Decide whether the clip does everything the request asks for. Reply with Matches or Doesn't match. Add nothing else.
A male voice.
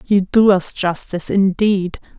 Doesn't match